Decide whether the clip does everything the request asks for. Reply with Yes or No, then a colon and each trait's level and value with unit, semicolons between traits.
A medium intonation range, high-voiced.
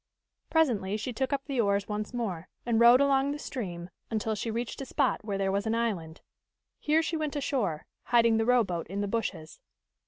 Yes: average, 4.9 semitones; high, 225 Hz